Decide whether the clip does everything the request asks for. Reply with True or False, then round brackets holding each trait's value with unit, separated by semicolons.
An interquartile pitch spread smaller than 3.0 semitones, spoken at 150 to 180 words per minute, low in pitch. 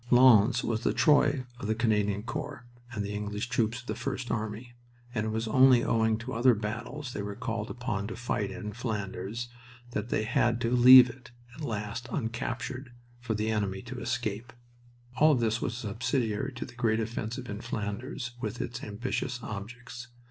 True (2.5 semitones; 175 wpm; 115 Hz)